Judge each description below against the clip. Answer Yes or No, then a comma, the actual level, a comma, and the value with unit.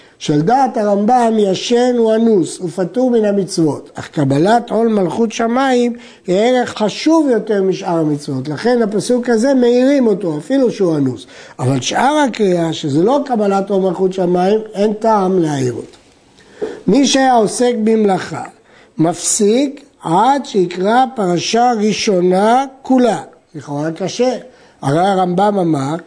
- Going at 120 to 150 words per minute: Yes, average, 130 wpm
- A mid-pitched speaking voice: No, high, 210 Hz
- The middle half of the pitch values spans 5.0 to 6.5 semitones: Yes, wide, 5.5 semitones